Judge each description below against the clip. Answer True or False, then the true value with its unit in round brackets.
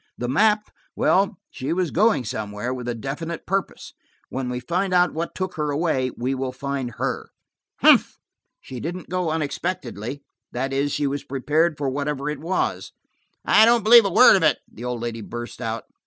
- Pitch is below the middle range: False (145 Hz)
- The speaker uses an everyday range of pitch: False (5.9 semitones)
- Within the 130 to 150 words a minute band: False (175 wpm)